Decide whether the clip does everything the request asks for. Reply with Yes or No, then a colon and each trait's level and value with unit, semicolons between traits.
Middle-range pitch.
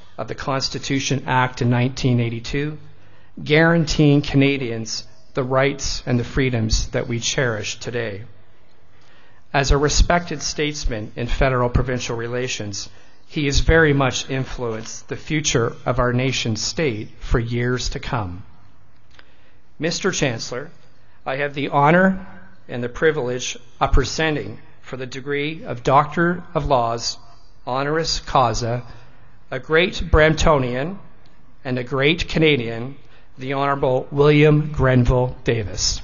No: low, 130 Hz